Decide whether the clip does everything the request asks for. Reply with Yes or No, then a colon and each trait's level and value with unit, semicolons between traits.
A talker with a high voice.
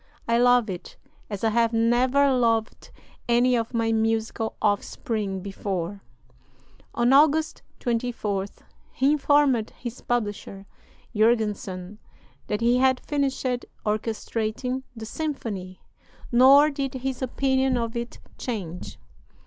Yes: high, 235 Hz